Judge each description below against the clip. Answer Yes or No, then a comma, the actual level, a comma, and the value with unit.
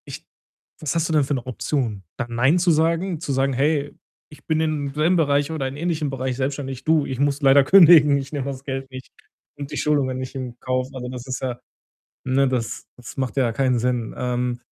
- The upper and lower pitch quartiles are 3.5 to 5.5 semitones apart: No, average, 2.8 semitones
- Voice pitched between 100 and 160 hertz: Yes, low, 135 Hz